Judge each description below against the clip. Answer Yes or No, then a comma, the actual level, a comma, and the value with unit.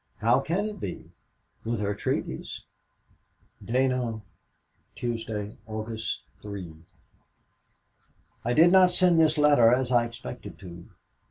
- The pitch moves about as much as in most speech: No, wide, 5.8 semitones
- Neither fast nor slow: No, slow, 110 wpm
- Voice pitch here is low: Yes, low, 120 Hz